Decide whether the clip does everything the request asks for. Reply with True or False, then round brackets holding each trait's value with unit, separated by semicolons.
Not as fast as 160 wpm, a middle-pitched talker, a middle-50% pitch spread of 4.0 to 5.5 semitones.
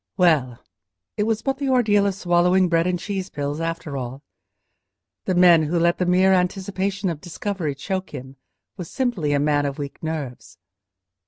False (170 wpm; 175 Hz; 4.5 semitones)